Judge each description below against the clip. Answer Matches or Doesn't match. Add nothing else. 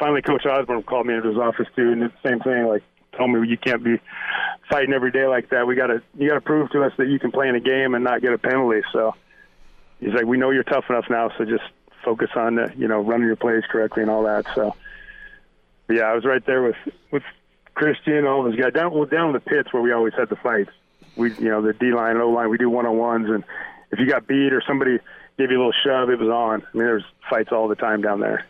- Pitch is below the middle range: Matches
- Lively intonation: Doesn't match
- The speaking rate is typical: Doesn't match